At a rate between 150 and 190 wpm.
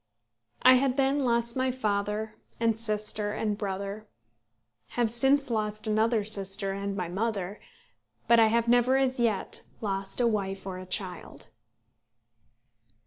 No: average, 140 wpm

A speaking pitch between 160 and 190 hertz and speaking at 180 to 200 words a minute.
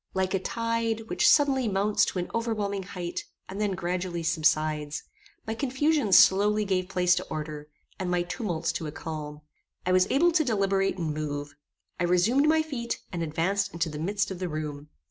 Yes: medium, 185 Hz; average, 185 wpm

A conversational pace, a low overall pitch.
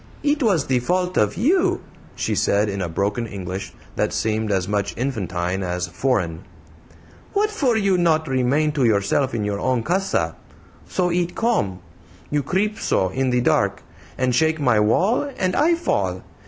Yes: average, 165 wpm; low, 130 Hz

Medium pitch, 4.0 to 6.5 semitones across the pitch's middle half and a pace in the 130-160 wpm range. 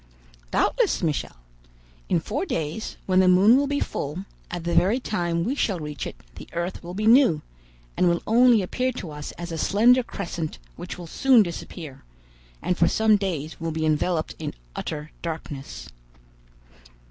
No: medium, 175 Hz; average, 5.3 semitones; average, 170 wpm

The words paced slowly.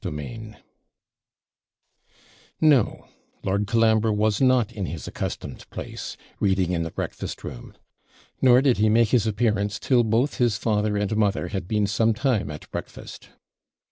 No: average, 145 wpm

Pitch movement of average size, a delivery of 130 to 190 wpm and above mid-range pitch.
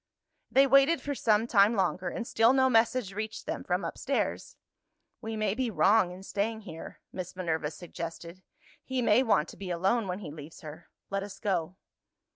Yes: average, 4.5 semitones; average, 180 wpm; high, 200 Hz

